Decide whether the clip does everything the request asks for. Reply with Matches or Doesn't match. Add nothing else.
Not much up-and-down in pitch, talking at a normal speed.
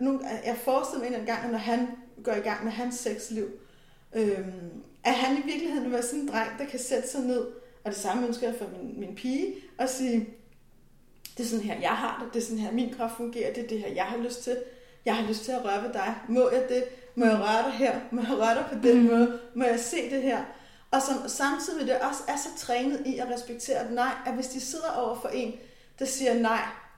Doesn't match